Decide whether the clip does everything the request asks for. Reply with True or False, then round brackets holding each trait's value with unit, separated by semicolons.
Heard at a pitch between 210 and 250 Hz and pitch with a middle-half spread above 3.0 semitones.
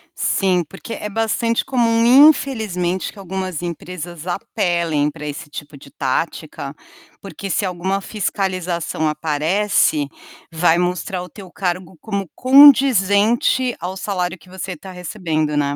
False (185 Hz; 3.5 semitones)